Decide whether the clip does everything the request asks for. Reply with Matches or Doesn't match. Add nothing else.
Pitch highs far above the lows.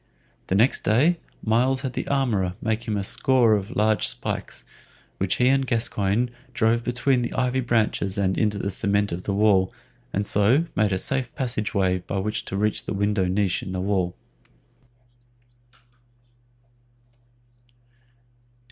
Doesn't match